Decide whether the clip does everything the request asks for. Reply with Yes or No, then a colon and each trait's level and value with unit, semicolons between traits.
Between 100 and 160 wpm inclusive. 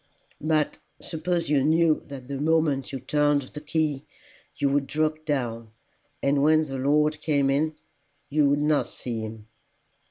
Yes: average, 155 wpm